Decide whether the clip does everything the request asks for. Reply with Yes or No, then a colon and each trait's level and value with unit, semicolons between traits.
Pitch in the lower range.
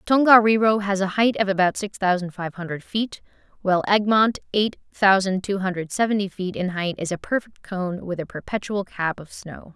No: high, 195 Hz